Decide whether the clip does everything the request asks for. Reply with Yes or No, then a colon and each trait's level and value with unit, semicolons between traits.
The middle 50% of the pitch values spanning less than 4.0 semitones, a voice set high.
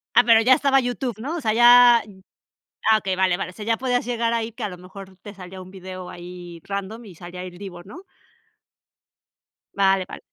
No: average, 4.3 semitones; high, 200 Hz